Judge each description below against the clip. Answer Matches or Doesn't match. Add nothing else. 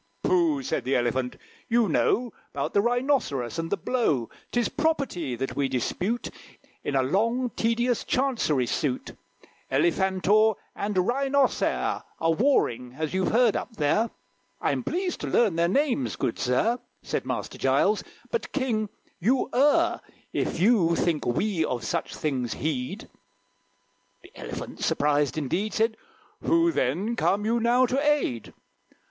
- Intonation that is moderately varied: Doesn't match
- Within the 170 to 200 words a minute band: Doesn't match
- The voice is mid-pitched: Doesn't match